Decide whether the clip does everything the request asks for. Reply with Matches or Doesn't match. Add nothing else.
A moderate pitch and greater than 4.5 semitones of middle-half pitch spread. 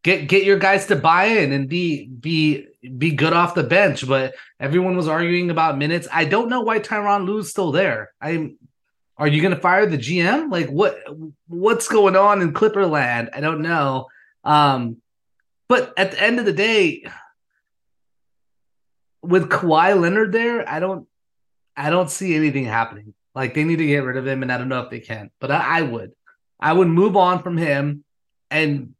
Matches